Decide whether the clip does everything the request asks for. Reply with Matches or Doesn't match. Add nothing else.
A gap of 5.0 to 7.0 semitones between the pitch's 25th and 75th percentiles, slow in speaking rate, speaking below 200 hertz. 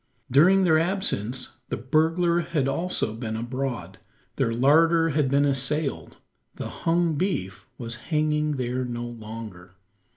Matches